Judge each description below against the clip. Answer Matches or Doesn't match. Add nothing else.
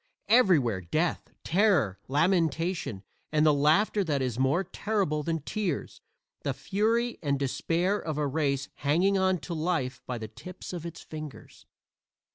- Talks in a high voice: Doesn't match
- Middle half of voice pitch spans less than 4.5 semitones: Doesn't match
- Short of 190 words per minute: Matches